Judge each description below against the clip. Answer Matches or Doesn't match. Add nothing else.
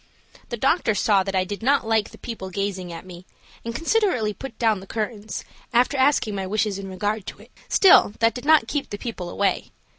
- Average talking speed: Doesn't match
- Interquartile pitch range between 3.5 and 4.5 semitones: Matches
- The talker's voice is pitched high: Matches